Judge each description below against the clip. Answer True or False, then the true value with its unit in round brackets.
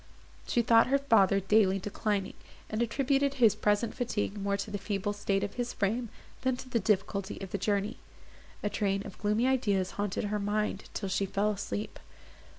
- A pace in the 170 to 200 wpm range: True (180 wpm)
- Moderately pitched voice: False (205 Hz)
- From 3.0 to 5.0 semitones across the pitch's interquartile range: False (2.6 semitones)